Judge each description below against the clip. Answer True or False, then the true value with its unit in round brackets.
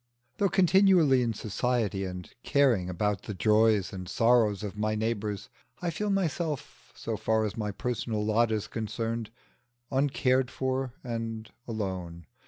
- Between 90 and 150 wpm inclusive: True (140 wpm)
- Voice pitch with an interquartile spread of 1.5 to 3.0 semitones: False (3.9 semitones)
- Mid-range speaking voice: False (115 Hz)